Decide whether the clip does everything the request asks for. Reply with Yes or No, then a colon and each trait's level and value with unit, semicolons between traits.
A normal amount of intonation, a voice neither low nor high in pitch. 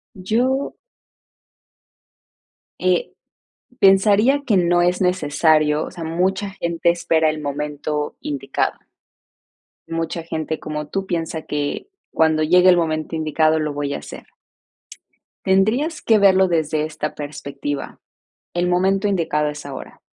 Yes: average, 3.7 semitones; medium, 165 Hz